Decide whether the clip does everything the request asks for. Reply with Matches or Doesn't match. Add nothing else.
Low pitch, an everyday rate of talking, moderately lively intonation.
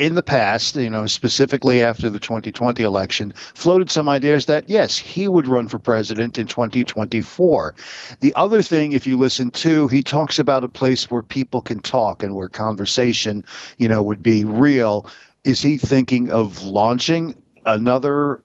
Matches